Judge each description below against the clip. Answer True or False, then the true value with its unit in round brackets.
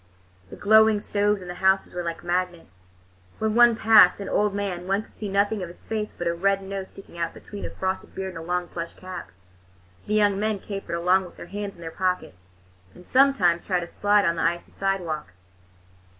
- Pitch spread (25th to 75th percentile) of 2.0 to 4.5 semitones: True (2.9 semitones)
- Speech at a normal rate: False (210 wpm)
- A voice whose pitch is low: False (190 Hz)